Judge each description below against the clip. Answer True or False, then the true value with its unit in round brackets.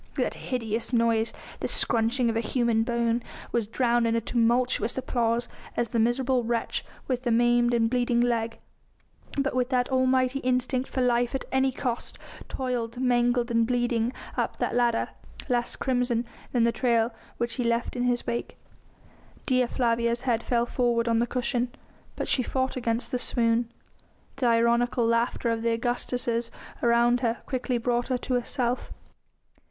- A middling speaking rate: True (160 wpm)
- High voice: True (240 Hz)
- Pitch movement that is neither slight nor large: False (1.2 semitones)